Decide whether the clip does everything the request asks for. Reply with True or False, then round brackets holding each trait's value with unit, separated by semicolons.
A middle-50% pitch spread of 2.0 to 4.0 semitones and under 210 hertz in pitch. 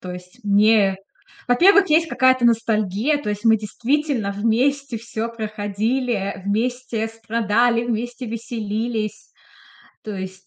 False (2.8 semitones; 225 Hz)